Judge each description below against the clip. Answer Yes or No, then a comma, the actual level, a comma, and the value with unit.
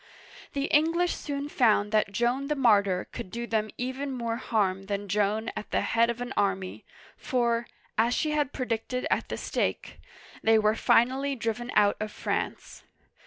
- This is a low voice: No, high, 235 Hz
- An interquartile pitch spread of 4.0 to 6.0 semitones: No, average, 3.6 semitones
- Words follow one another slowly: No, average, 165 wpm